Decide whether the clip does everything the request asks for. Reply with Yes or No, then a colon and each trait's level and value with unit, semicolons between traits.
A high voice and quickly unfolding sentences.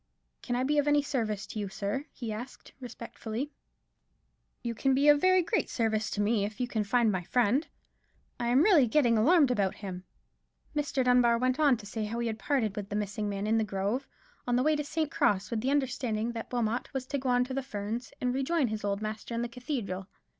Yes: high, 240 Hz; fast, 225 wpm